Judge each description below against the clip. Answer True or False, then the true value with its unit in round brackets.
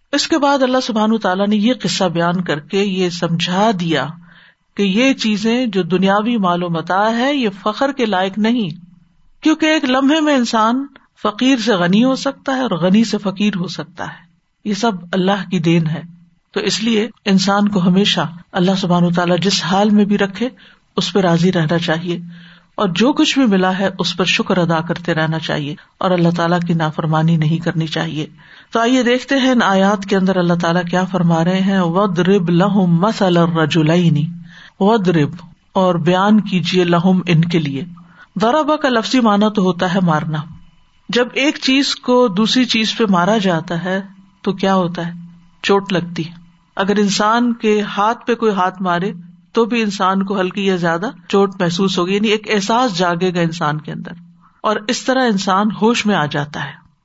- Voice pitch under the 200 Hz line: True (190 Hz)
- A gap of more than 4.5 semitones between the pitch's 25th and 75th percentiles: False (4.0 semitones)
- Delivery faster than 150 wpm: True (185 wpm)